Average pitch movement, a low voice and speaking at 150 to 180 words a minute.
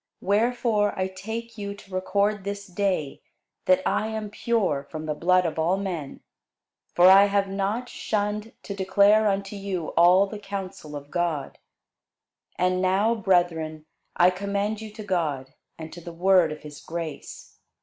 No: average, 3.0 semitones; high, 190 Hz; average, 160 wpm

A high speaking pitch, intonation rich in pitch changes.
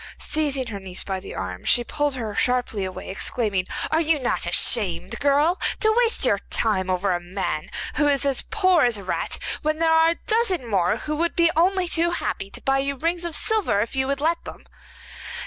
Yes: very high, 275 Hz; wide, 8.6 semitones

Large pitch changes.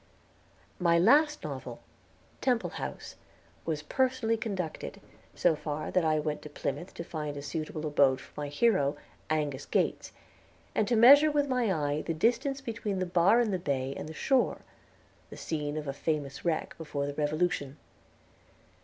Yes: wide, 7.3 semitones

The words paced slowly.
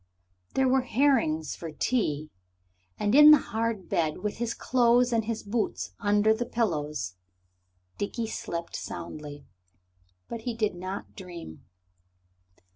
Yes: slow, 125 wpm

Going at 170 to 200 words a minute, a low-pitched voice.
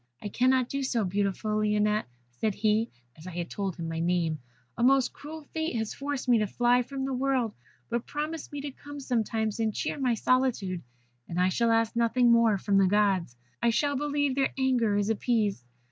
No: average, 195 wpm; high, 230 Hz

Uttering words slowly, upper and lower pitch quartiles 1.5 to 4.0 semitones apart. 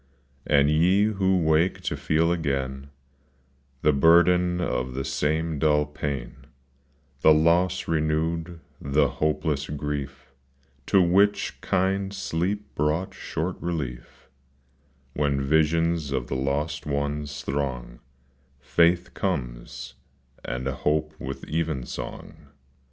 Yes: slow, 110 wpm; average, 3.5 semitones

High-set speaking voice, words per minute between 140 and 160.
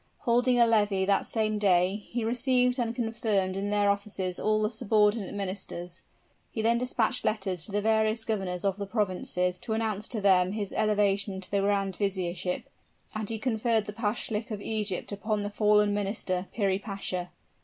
No: high, 205 Hz; average, 170 wpm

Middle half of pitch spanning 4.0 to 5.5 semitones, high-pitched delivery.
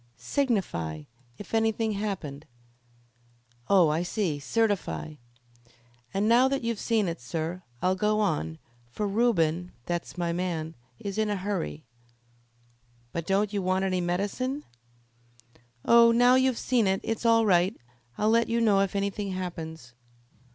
Yes: average, 4.5 semitones; high, 195 Hz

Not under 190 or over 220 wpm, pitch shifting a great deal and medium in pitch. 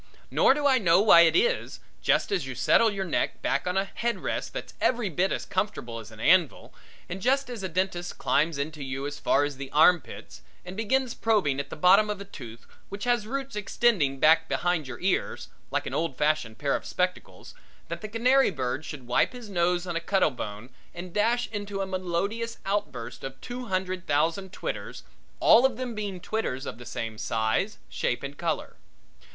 Yes: average, 200 wpm; wide, 6.7 semitones; medium, 180 Hz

